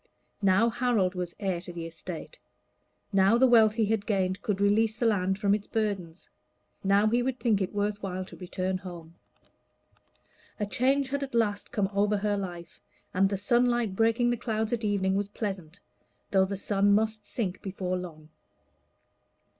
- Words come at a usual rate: Yes, average, 165 wpm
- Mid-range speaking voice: No, high, 205 Hz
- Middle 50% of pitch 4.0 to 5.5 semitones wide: No, average, 2.9 semitones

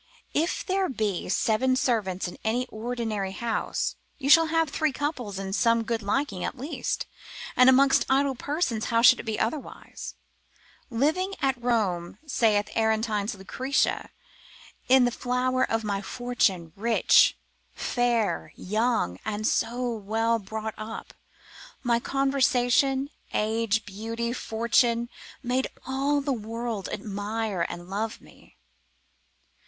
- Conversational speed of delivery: No, slow, 125 wpm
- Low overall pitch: No, high, 235 Hz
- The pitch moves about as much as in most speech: Yes, average, 3.3 semitones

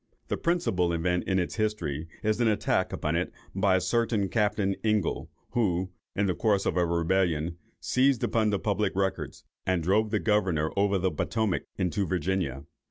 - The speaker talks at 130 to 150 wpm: No, average, 170 wpm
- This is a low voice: Yes, very low, 95 Hz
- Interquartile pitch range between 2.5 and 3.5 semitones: Yes, average, 3.2 semitones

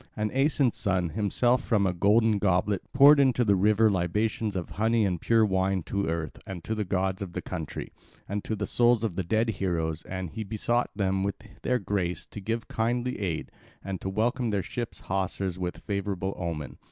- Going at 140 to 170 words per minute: No, average, 190 wpm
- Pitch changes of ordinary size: Yes, average, 3.3 semitones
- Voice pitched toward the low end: Yes, low, 100 Hz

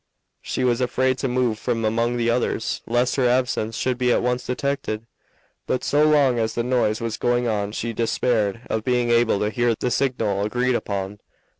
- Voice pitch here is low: Yes, low, 120 Hz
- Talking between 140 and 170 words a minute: No, average, 190 wpm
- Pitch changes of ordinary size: No, narrow, 2.1 semitones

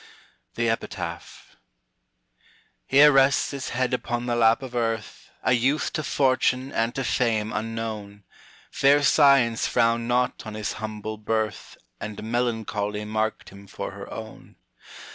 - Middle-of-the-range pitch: No, low, 115 Hz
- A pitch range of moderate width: Yes, average, 3.0 semitones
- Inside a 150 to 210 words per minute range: No, slow, 135 wpm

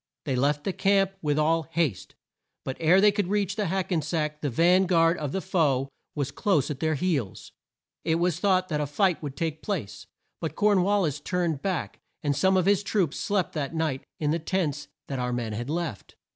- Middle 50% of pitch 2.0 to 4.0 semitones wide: No, average, 4.4 semitones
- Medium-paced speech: No, fast, 215 wpm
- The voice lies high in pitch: No, medium, 165 Hz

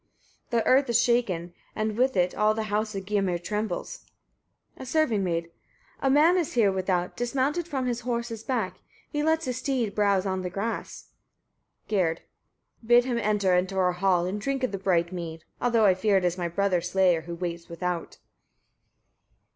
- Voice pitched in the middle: No, high, 205 Hz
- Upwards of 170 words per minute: Yes, average, 185 wpm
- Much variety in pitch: No, average, 5.0 semitones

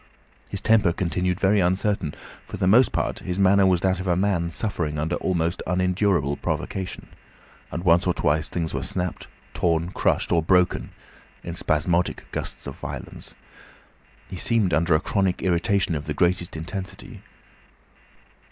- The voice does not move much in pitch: Yes, narrow, 2.3 semitones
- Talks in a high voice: No, very low, 90 Hz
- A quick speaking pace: No, average, 150 wpm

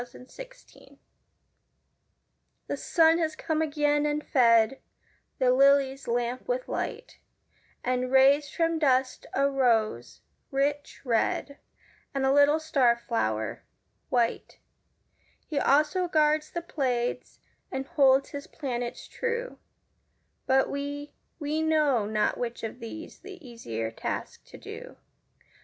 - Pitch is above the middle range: Yes, very high, 275 Hz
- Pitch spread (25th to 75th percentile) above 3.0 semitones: Yes, average, 3.9 semitones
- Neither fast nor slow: No, slow, 120 wpm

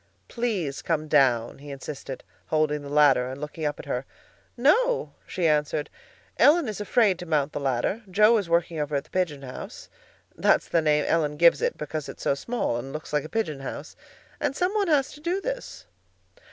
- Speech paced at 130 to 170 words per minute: No, average, 190 wpm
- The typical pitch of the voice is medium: Yes, medium, 155 Hz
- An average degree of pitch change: No, wide, 7.0 semitones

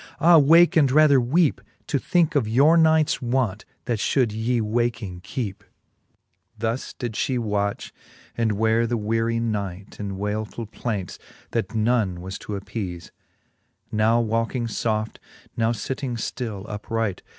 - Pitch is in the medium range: No, low, 115 Hz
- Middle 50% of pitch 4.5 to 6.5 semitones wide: No, average, 3.1 semitones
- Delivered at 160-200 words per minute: No, average, 140 wpm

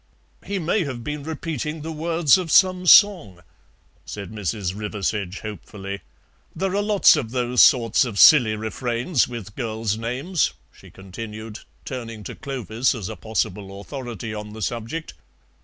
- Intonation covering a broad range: Yes, wide, 6.3 semitones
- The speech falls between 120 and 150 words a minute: Yes, average, 145 wpm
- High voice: No, low, 115 Hz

